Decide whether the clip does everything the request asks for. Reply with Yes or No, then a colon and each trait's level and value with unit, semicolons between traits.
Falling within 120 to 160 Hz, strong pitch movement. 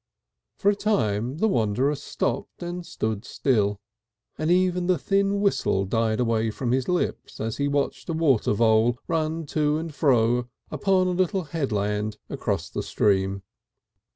Yes: low, 135 Hz; wide, 7.9 semitones